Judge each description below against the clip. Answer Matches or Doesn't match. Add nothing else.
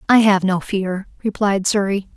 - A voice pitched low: Doesn't match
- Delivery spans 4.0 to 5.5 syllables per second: Matches